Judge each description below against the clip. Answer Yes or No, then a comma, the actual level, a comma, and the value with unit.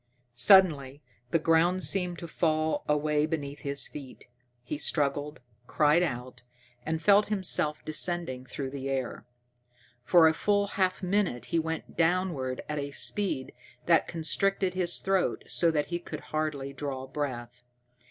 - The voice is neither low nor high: Yes, medium, 155 Hz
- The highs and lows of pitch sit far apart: No, average, 3.8 semitones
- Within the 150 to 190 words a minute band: No, average, 140 wpm